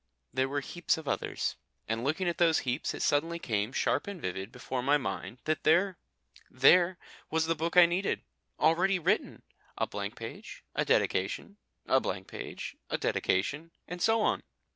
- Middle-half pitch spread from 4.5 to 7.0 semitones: Yes, average, 5.1 semitones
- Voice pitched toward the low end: No, medium, 160 Hz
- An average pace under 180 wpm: Yes, average, 170 wpm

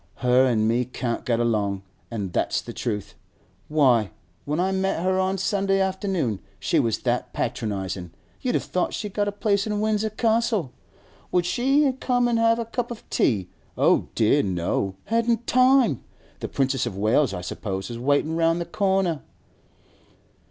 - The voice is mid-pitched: Yes, medium, 160 Hz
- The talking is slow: No, average, 165 wpm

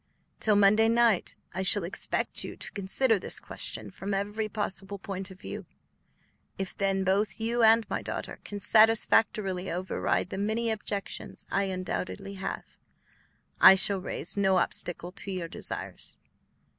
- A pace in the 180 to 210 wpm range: No, average, 145 wpm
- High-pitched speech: Yes, high, 200 Hz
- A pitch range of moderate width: No, narrow, 2.3 semitones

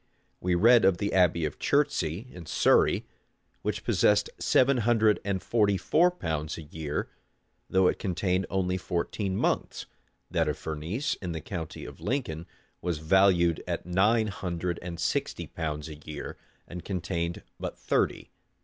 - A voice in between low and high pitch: No, very low, 90 Hz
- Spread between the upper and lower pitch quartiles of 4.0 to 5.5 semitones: No, average, 3.6 semitones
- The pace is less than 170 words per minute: Yes, average, 150 wpm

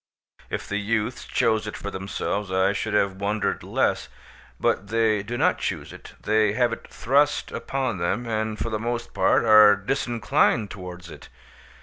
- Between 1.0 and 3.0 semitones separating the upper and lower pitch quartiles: Yes, narrow, 2.4 semitones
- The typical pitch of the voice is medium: No, low, 110 Hz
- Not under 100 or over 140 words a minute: No, average, 165 wpm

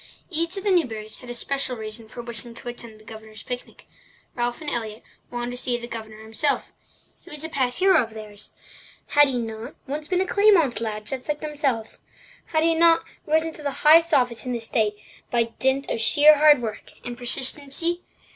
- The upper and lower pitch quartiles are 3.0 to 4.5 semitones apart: No, average, 5.1 semitones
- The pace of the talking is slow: No, average, 200 wpm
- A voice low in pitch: No, high, 245 Hz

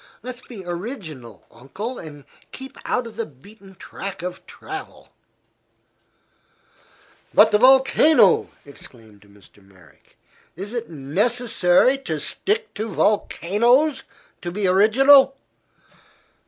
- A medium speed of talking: No, slow, 105 wpm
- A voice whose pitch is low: No, high, 205 Hz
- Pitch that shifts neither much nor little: No, wide, 8.0 semitones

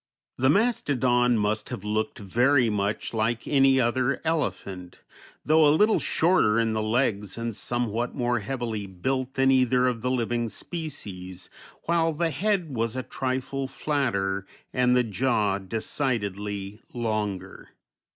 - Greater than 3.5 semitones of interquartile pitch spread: Yes, average, 4.1 semitones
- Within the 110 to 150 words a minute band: Yes, slow, 135 wpm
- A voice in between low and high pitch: No, low, 120 Hz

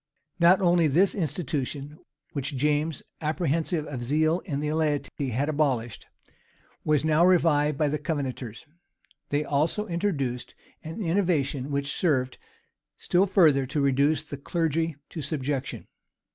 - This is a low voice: No, medium, 150 Hz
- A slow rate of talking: Yes, slow, 130 wpm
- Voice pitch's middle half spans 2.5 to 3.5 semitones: Yes, average, 2.9 semitones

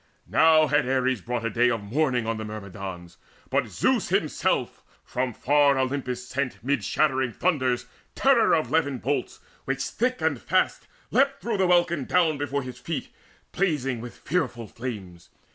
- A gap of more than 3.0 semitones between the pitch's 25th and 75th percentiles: Yes, average, 4.4 semitones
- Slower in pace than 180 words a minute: Yes, average, 160 wpm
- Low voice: Yes, low, 130 Hz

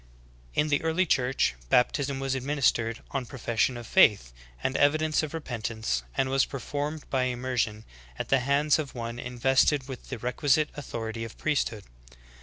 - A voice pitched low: Yes, low, 130 Hz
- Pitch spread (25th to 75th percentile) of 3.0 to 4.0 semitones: Yes, average, 3.3 semitones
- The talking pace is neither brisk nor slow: Yes, average, 155 wpm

